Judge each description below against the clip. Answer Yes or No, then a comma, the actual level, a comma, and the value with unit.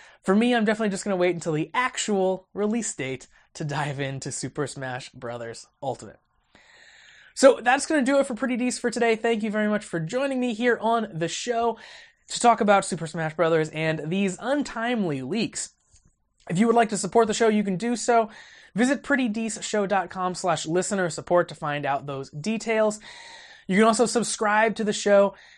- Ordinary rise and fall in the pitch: No, wide, 5.7 semitones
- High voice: Yes, high, 210 Hz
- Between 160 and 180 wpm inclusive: No, average, 190 wpm